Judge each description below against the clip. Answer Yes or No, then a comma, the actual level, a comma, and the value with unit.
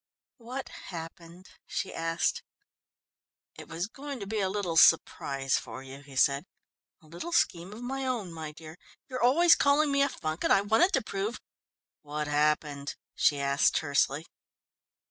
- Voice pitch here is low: No, medium, 170 Hz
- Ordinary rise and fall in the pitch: No, wide, 8.1 semitones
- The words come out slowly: No, average, 165 wpm